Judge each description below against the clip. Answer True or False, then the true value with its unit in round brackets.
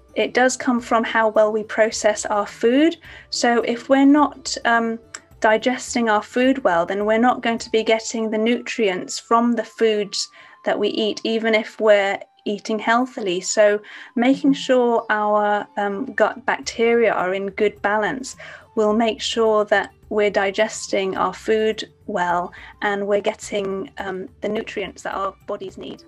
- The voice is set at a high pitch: True (220 Hz)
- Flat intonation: True (2.2 semitones)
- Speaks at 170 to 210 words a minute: False (160 wpm)